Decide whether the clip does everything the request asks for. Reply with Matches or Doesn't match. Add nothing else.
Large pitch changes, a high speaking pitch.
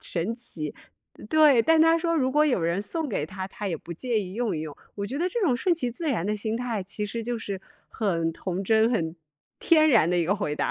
Matches